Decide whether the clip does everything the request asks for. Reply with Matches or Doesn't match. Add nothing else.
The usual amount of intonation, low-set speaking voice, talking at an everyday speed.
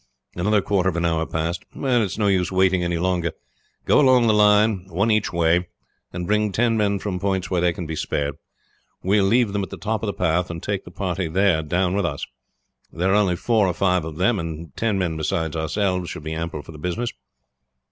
Doesn't match